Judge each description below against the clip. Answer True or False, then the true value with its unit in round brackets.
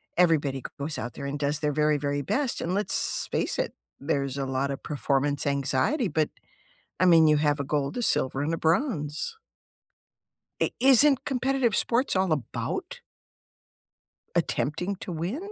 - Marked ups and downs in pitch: True (5.7 semitones)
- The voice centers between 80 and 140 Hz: False (150 Hz)